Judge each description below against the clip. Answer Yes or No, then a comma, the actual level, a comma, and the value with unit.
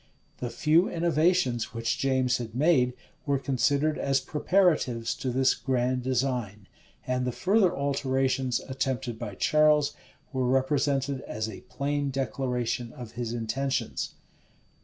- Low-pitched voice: Yes, low, 130 Hz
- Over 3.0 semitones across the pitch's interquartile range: No, average, 2.7 semitones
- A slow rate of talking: Yes, slow, 130 wpm